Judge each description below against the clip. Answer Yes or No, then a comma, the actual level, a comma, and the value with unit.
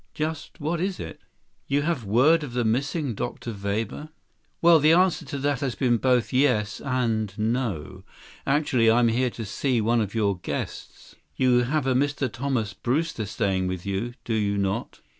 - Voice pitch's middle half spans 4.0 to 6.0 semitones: Yes, average, 4.9 semitones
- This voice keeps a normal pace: Yes, average, 180 wpm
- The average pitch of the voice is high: No, low, 120 Hz